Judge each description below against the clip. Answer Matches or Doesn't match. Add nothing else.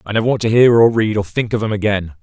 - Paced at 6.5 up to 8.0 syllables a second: Matches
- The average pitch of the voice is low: Matches